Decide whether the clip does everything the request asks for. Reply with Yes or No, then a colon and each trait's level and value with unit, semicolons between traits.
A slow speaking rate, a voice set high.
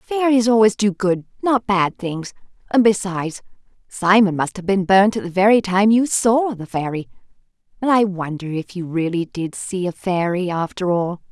No: average, 180 wpm; high, 195 Hz